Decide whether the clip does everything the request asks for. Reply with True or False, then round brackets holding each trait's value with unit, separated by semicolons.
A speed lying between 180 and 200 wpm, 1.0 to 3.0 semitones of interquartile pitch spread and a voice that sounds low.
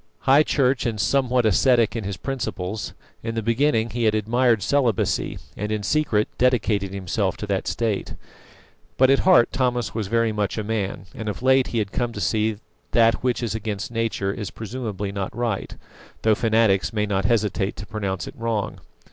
True (185 wpm; 2.7 semitones; 110 Hz)